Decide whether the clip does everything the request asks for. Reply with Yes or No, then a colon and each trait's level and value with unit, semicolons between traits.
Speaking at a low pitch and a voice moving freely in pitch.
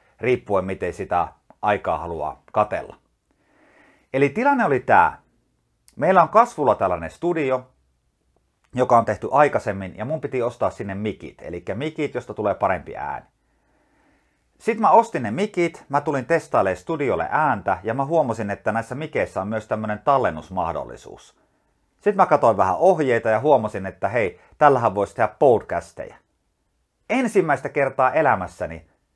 Yes: low, 130 Hz; wide, 6.5 semitones